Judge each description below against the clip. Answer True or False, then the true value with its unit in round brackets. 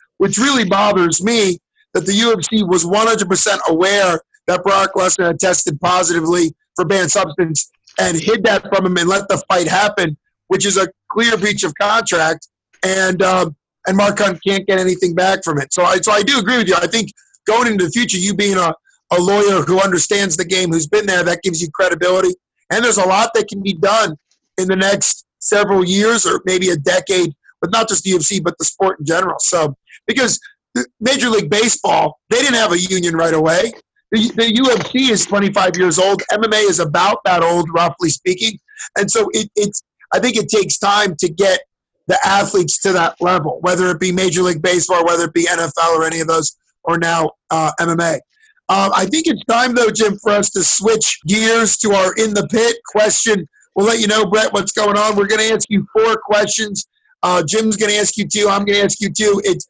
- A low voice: False (195 Hz)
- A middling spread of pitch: True (3.0 semitones)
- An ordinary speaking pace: False (215 wpm)